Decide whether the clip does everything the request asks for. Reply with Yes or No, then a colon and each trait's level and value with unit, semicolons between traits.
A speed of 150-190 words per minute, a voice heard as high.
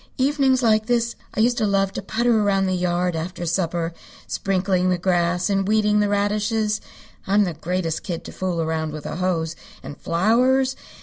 Yes: average, 180 wpm; high, 195 Hz